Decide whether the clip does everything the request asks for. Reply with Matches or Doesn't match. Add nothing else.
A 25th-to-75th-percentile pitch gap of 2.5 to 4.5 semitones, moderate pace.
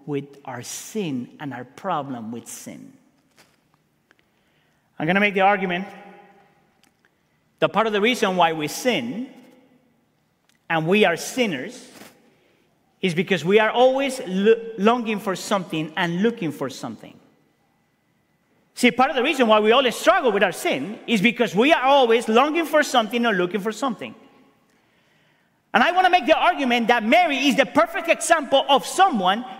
Doesn't match